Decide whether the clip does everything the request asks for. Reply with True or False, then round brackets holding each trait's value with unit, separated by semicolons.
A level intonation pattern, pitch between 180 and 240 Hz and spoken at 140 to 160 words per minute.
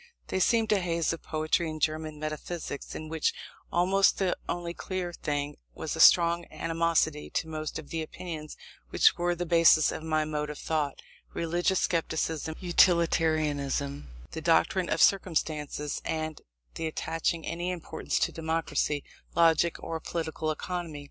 False (1.9 semitones; 160 Hz; 150 wpm)